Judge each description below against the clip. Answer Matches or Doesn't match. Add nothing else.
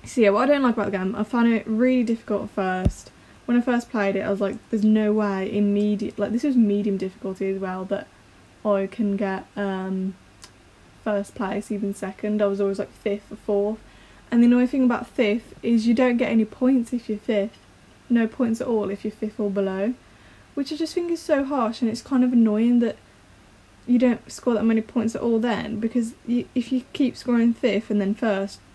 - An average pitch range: Matches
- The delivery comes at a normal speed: Doesn't match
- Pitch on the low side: Doesn't match